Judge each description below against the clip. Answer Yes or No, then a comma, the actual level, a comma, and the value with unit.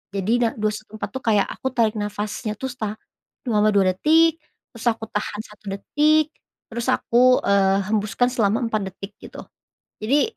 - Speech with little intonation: No, average, 3.1 semitones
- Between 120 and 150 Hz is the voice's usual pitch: No, high, 215 Hz